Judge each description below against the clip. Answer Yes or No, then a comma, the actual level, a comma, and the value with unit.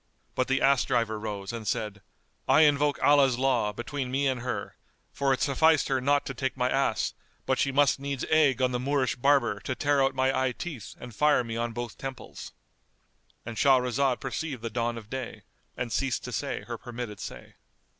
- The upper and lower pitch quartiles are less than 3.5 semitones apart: Yes, average, 2.7 semitones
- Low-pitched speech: Yes, low, 130 Hz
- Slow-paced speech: No, average, 195 wpm